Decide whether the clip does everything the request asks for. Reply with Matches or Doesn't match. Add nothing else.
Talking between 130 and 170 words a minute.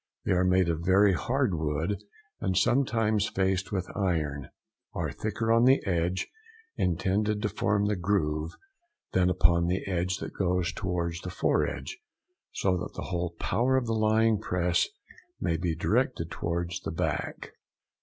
Matches